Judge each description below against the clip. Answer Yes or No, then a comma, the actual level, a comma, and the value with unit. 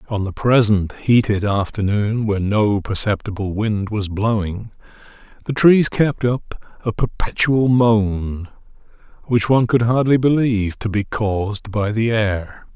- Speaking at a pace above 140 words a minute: No, slow, 135 wpm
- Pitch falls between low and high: No, low, 110 Hz